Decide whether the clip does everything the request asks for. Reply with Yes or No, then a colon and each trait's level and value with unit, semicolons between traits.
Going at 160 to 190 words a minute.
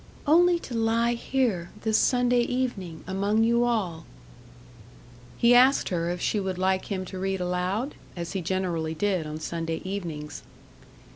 No: average, 150 wpm